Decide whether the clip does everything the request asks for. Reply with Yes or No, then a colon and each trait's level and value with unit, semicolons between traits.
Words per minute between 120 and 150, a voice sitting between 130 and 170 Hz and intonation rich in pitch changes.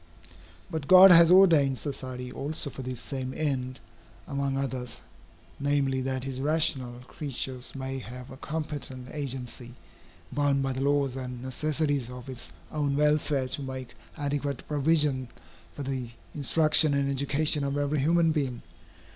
No: average, 140 wpm; medium, 140 Hz; narrow, 2.4 semitones